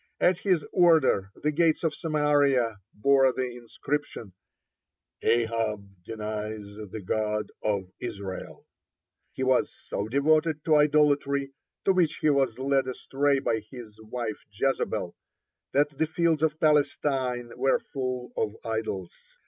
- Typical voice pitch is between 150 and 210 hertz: No, low, 130 Hz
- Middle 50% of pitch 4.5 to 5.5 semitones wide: Yes, average, 5.2 semitones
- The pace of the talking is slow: Yes, slow, 125 wpm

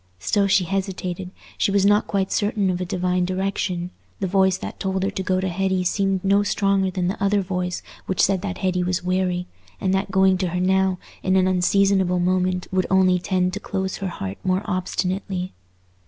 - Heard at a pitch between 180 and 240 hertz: Yes, medium, 185 Hz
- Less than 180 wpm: No, average, 200 wpm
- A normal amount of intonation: No, narrow, 1.1 semitones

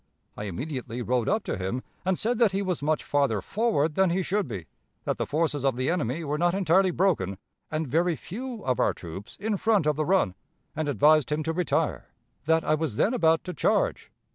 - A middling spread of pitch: No, wide, 6.0 semitones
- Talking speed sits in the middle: No, fast, 215 wpm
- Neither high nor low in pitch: Yes, medium, 155 Hz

